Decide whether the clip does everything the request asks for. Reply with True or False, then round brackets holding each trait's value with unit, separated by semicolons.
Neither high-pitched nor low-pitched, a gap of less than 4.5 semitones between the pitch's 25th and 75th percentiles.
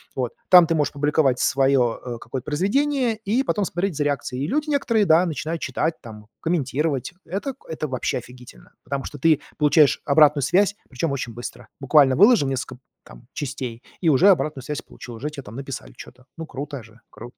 False (145 Hz; 4.8 semitones)